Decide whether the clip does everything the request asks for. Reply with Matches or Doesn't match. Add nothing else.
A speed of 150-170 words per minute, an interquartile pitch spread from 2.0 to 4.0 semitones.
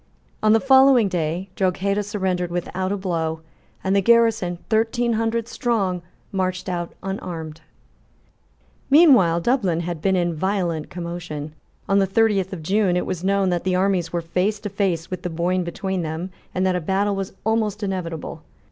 Matches